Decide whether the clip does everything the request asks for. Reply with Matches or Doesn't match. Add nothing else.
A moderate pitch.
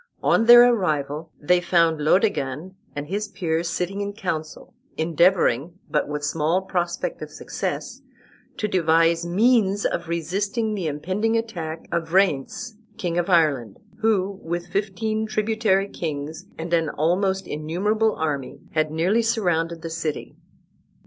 Matches